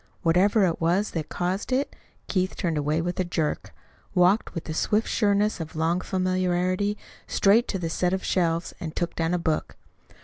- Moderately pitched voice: Yes, medium, 180 Hz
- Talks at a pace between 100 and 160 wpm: No, average, 180 wpm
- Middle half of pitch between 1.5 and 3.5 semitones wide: Yes, average, 2.8 semitones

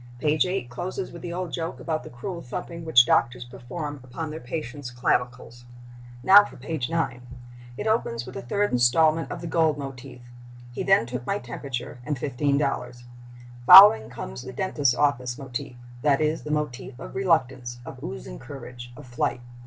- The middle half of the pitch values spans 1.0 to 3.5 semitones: No, average, 4.7 semitones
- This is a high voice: No, low, 130 Hz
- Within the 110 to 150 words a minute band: No, average, 165 wpm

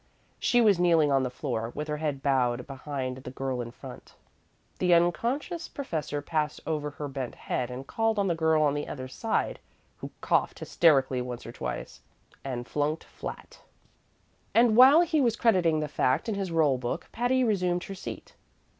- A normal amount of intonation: No, wide, 6.8 semitones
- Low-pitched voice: No, medium, 150 Hz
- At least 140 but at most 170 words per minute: No, average, 180 wpm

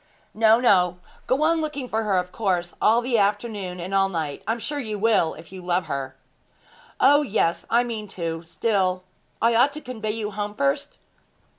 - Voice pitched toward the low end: No, high, 210 Hz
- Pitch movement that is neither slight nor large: Yes, average, 4.5 semitones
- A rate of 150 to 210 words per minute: Yes, average, 190 wpm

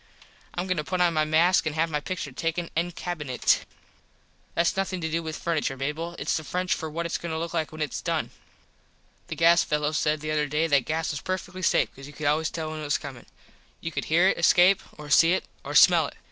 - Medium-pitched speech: Yes, medium, 160 Hz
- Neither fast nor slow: No, fast, 245 wpm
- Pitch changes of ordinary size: No, narrow, 2.2 semitones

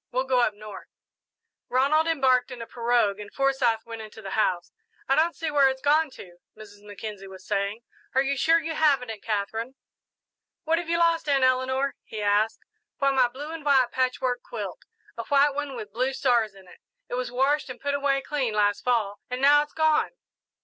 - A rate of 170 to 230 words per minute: Yes, average, 200 wpm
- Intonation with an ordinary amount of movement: Yes, average, 4.6 semitones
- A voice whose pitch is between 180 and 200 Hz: No, very high, 255 Hz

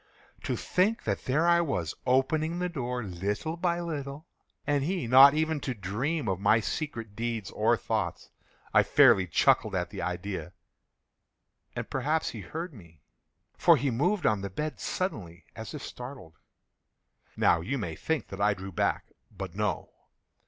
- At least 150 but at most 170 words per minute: Yes, average, 160 wpm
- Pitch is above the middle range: No, low, 125 Hz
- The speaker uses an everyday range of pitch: No, wide, 8.2 semitones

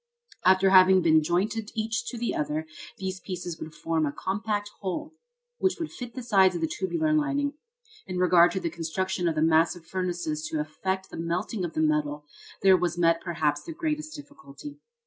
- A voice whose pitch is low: No, medium, 185 Hz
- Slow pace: No, average, 185 wpm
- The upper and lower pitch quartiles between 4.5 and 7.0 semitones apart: Yes, wide, 5.5 semitones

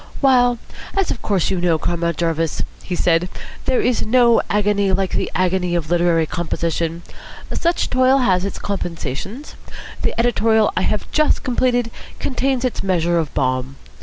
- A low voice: No, high, 190 Hz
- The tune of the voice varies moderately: No, wide, 6.3 semitones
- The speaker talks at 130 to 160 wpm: Yes, average, 155 wpm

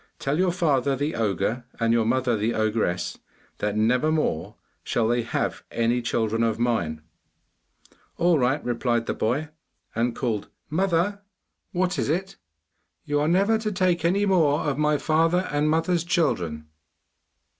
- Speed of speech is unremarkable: Yes, average, 155 wpm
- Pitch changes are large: Yes, wide, 6.5 semitones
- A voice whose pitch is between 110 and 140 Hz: Yes, low, 135 Hz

